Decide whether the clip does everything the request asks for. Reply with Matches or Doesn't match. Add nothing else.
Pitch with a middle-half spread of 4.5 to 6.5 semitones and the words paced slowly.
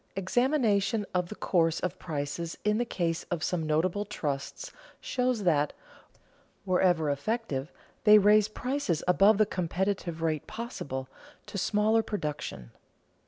Matches